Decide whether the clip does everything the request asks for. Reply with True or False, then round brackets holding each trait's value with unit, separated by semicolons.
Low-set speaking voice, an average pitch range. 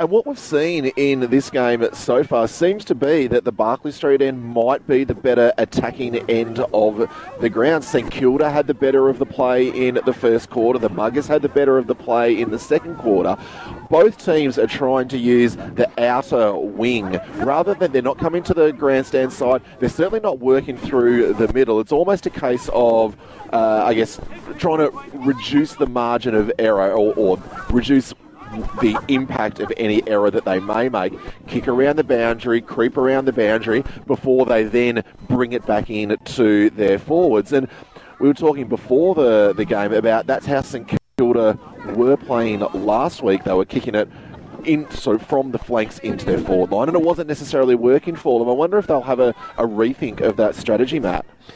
True (125 Hz; 3.2 semitones)